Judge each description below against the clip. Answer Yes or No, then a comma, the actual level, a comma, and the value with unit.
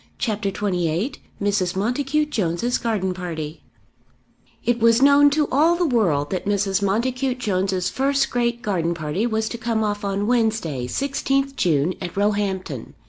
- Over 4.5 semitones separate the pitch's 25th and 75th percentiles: Yes, average, 5.1 semitones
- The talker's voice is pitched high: Yes, high, 210 Hz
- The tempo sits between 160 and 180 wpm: No, average, 145 wpm